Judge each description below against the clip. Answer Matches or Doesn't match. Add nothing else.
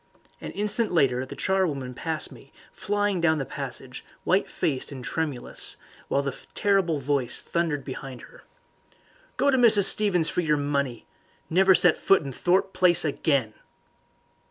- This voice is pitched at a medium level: Matches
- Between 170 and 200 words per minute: Doesn't match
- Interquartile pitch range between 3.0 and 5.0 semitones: Doesn't match